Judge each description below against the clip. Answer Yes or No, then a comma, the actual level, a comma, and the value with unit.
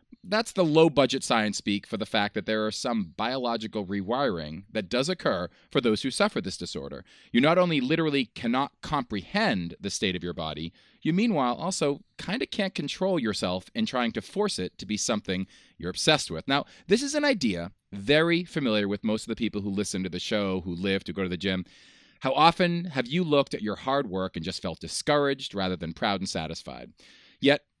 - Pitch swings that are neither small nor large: No, wide, 8.9 semitones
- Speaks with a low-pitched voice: Yes, low, 110 Hz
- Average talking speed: No, fast, 210 wpm